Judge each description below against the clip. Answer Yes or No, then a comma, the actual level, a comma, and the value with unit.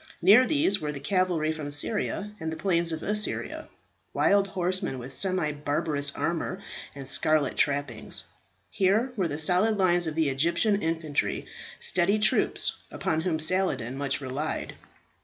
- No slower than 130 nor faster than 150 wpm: Yes, average, 145 wpm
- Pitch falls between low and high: Yes, medium, 165 Hz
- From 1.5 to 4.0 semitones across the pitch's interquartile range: No, average, 4.7 semitones